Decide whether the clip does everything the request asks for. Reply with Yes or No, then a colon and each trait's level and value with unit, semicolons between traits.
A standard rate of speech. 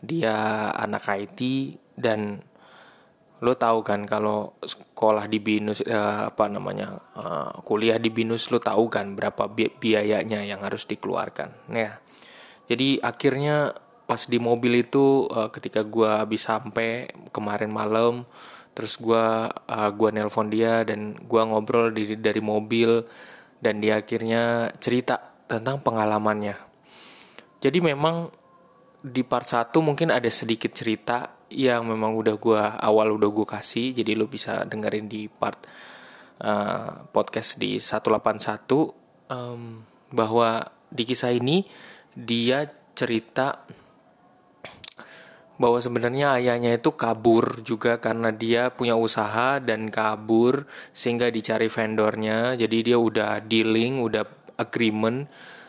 Yes: average, 125 wpm